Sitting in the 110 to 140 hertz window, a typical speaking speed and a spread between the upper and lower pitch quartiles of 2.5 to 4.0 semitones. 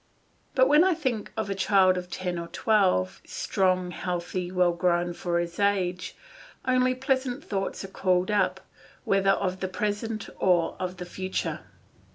No: medium, 185 Hz; average, 155 wpm; average, 2.8 semitones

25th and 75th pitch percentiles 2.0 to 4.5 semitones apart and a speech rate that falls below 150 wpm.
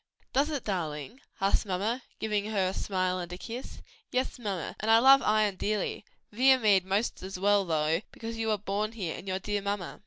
No: average, 3.1 semitones; average, 195 wpm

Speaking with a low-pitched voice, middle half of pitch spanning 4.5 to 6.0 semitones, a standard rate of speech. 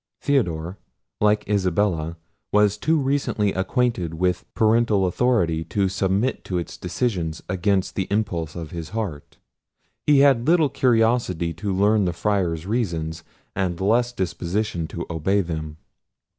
No: very low, 95 Hz; average, 4.8 semitones; slow, 130 wpm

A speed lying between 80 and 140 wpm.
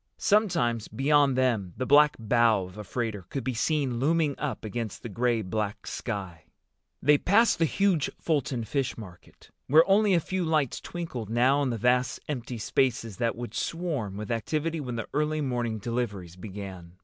No: average, 175 wpm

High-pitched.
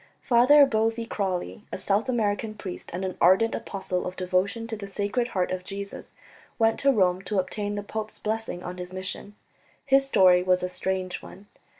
Yes: high, 200 Hz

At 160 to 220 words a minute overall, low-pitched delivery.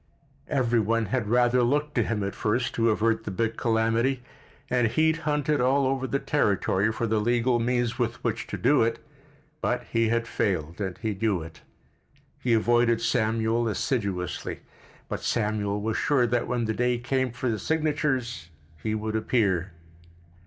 Yes: average, 170 wpm; low, 115 Hz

